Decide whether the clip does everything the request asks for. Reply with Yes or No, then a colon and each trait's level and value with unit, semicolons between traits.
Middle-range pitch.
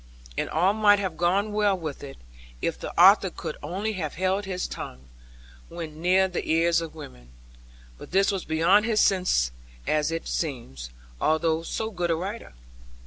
Yes: medium, 175 Hz